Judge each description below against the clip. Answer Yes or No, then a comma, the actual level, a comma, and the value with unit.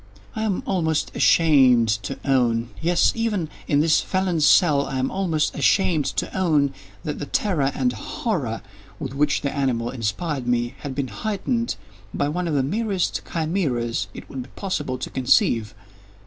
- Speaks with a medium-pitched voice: Yes, medium, 145 Hz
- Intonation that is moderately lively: No, wide, 5.9 semitones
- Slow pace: No, average, 155 wpm